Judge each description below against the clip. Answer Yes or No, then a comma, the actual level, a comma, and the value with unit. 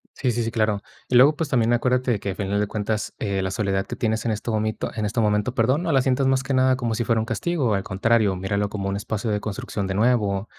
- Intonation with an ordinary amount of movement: Yes, average, 3.5 semitones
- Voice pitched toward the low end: Yes, low, 110 Hz